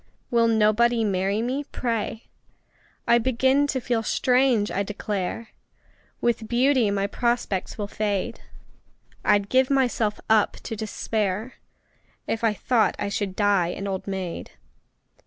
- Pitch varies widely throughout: No, average, 3.0 semitones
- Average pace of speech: No, slow, 130 wpm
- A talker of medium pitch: No, high, 220 Hz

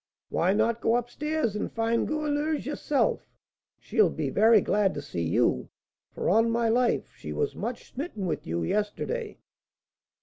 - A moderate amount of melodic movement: No, wide, 5.9 semitones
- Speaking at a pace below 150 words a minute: No, average, 160 wpm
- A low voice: No, high, 230 Hz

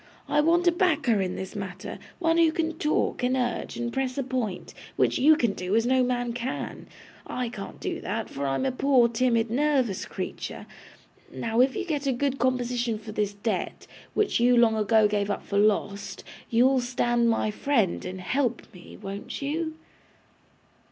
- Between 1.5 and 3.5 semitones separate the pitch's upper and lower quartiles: No, average, 4.2 semitones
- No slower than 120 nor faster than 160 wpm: No, average, 185 wpm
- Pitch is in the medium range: No, high, 240 Hz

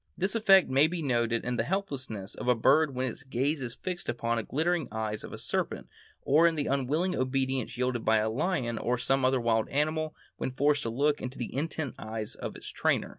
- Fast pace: Yes, fast, 220 wpm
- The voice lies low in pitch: Yes, low, 130 Hz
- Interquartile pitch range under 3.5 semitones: No, average, 4.8 semitones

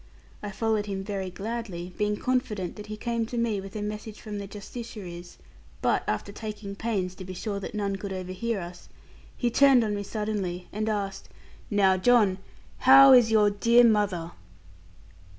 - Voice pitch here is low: No, high, 210 Hz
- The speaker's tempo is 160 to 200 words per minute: Yes, average, 170 wpm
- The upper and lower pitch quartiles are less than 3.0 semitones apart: Yes, narrow, 2.6 semitones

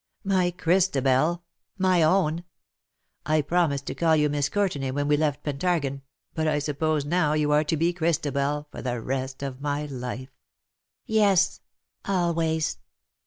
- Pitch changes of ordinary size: Yes, average, 3.5 semitones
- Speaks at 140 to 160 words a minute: Yes, average, 155 wpm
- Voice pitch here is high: No, medium, 150 Hz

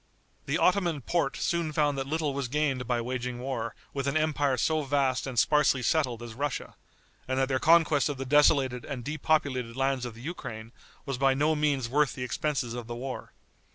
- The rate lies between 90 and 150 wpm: No, average, 195 wpm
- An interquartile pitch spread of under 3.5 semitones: Yes, average, 3.0 semitones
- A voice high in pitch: No, low, 135 Hz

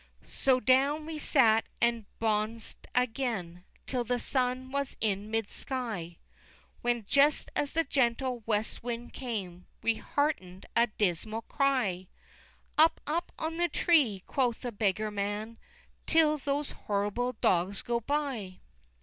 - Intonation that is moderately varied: Yes, average, 4.7 semitones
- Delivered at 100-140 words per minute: Yes, slow, 135 wpm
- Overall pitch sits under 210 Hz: No, high, 235 Hz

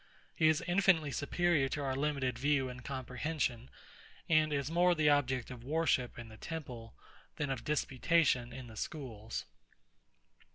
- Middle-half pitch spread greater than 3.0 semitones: Yes, average, 3.7 semitones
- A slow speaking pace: No, average, 150 wpm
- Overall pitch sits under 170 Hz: Yes, medium, 140 Hz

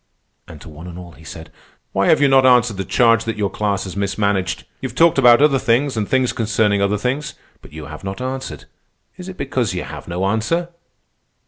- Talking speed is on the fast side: Yes, fast, 220 wpm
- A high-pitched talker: No, low, 105 Hz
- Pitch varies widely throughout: Yes, wide, 5.7 semitones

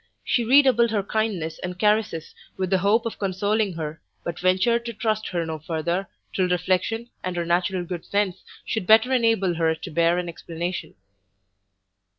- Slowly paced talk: No, average, 165 wpm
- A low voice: No, medium, 185 Hz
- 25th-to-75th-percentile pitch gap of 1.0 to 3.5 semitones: No, average, 4.1 semitones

